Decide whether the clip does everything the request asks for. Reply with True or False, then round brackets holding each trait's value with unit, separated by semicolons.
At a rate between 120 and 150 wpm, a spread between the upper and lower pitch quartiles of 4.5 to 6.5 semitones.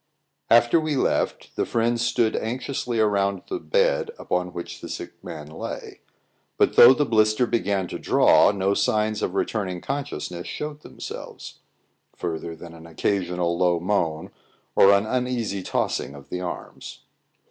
True (145 wpm; 5.2 semitones)